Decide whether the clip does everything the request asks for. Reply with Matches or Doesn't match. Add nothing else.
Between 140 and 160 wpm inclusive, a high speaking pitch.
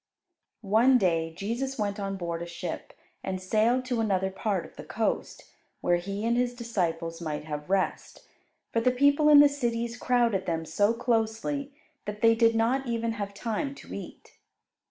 Doesn't match